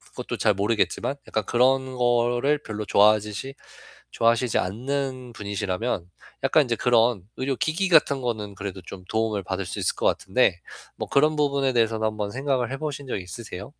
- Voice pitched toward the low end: Yes, low, 120 Hz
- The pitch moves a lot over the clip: No, average, 4.3 semitones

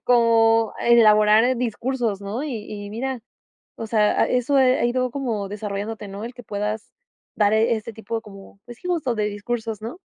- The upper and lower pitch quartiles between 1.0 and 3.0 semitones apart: Yes, narrow, 2.6 semitones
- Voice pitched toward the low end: No, high, 225 Hz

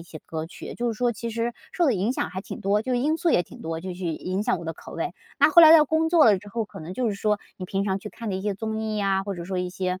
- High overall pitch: Yes, high, 205 Hz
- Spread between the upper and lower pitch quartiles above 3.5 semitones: Yes, average, 4.3 semitones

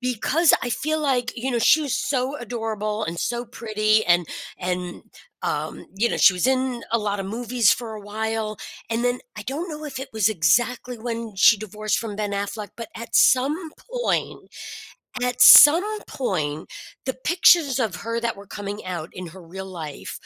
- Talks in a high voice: Yes, high, 225 Hz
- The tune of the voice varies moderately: Yes, average, 3.8 semitones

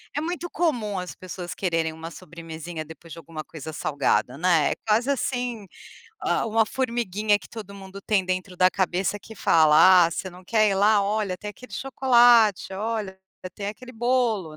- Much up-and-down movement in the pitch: No, average, 4.4 semitones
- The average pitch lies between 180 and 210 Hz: Yes, high, 195 Hz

